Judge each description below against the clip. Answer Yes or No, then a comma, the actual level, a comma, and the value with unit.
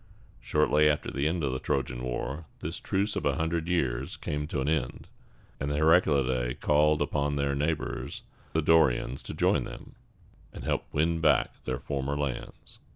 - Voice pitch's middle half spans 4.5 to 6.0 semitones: No, average, 2.9 semitones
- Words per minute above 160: Yes, average, 175 wpm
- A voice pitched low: Yes, very low, 75 Hz